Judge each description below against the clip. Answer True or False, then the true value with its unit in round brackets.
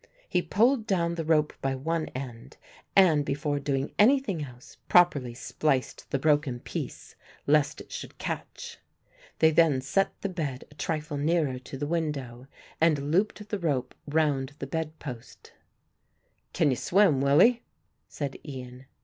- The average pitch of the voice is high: False (150 Hz)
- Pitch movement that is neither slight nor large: True (3.7 semitones)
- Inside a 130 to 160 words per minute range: True (150 wpm)